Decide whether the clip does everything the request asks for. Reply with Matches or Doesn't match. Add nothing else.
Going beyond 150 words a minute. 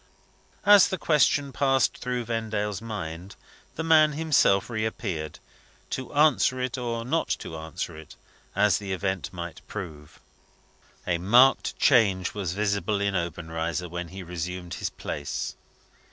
Doesn't match